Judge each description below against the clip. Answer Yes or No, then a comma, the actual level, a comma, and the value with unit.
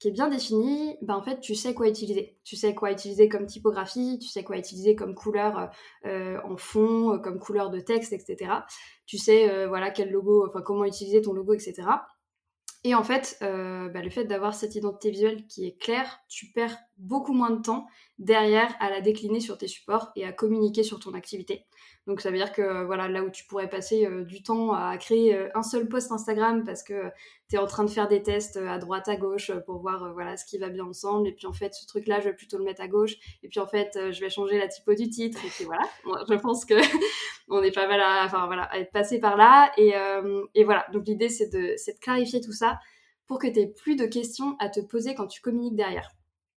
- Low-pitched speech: No, high, 210 Hz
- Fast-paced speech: Yes, fast, 245 wpm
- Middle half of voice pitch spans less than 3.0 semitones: Yes, narrow, 2.4 semitones